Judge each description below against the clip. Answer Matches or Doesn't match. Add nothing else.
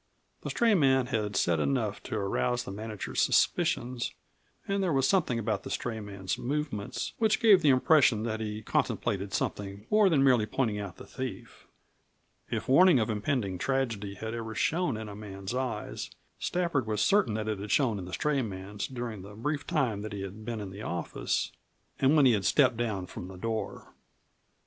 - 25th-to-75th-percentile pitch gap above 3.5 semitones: Matches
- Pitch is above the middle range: Doesn't match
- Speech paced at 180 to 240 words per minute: Matches